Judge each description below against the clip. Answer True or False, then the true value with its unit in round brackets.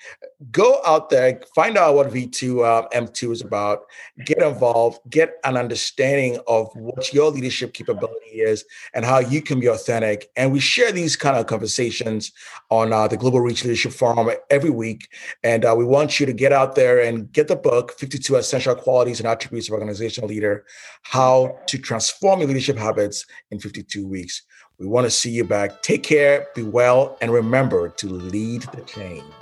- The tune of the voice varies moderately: True (3.9 semitones)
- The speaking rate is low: False (190 wpm)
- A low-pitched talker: True (125 Hz)